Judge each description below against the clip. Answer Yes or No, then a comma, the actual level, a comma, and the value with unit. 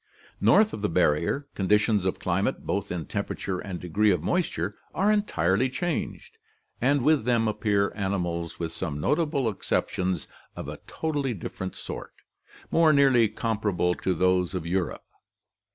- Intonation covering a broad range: Yes, wide, 6.8 semitones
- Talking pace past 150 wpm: No, average, 145 wpm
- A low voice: Yes, low, 100 Hz